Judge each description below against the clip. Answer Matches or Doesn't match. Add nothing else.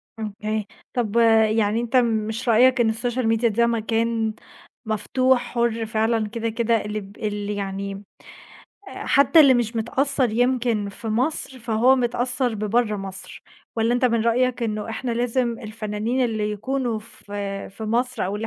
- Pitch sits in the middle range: Doesn't match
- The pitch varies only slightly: Matches